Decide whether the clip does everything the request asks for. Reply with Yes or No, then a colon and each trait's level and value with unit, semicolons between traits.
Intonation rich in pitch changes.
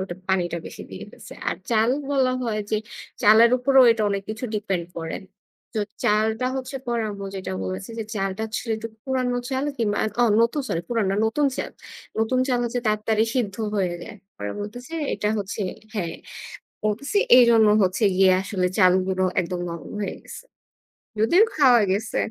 No: average, 4.1 semitones